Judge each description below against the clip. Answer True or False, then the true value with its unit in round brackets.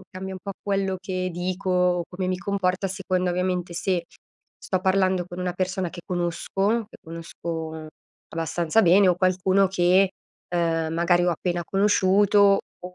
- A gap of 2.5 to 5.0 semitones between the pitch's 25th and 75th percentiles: False (1.6 semitones)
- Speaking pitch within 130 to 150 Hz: False (185 Hz)